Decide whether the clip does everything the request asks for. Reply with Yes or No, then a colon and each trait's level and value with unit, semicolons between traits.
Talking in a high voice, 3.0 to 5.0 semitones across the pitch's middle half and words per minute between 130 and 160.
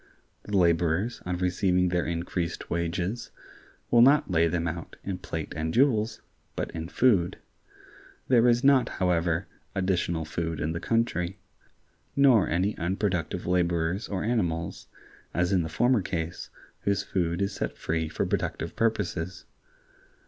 No: very low, 90 Hz; average, 3.6 semitones; average, 140 wpm